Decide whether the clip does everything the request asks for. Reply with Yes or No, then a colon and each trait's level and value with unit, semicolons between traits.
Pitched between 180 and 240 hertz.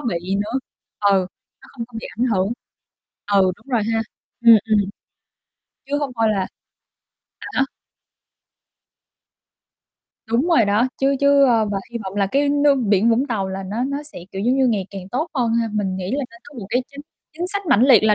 Yes: high, 230 Hz